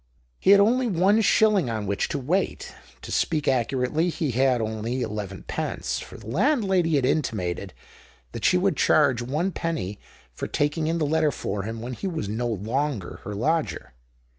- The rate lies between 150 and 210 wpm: Yes, average, 170 wpm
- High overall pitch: No, medium, 140 Hz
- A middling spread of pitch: No, wide, 7.0 semitones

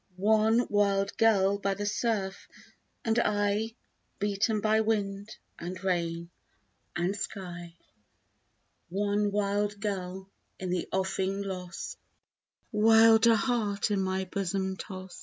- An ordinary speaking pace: No, slow, 110 wpm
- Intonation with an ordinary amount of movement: No, narrow, 1.9 semitones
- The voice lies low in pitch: No, high, 200 Hz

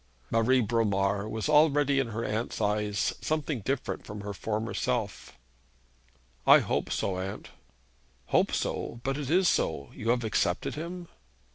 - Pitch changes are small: No, average, 5.2 semitones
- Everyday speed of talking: Yes, average, 145 wpm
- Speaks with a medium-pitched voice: No, low, 115 Hz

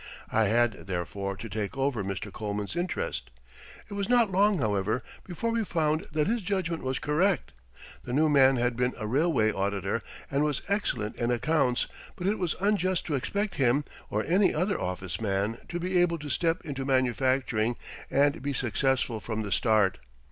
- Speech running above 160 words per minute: Yes, average, 175 wpm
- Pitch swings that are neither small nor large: No, wide, 8.0 semitones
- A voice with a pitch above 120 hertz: Yes, low, 135 Hz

